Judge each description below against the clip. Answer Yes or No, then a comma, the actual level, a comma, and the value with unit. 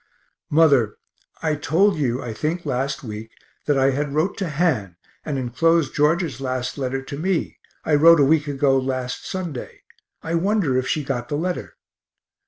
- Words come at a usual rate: Yes, average, 170 wpm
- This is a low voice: No, medium, 145 Hz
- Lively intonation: No, average, 3.9 semitones